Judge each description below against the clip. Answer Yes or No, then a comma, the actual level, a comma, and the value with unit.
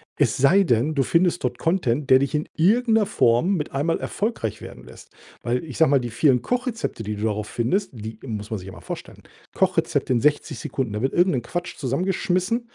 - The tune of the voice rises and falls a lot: Yes, wide, 7.3 semitones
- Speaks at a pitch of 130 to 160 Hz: Yes, medium, 140 Hz